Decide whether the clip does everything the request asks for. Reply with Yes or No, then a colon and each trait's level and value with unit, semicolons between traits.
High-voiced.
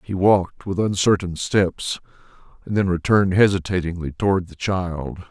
No: very low, 95 Hz